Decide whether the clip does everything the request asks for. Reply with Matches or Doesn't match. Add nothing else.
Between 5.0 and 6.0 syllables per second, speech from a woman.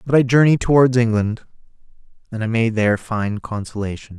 Doesn't match